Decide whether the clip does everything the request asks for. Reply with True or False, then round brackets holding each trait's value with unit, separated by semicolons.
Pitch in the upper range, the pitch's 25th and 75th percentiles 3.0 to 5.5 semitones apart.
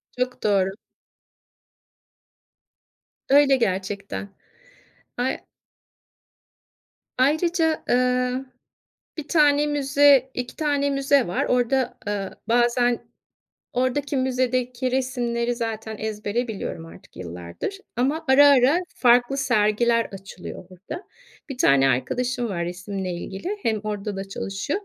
True (245 Hz; 4.7 semitones)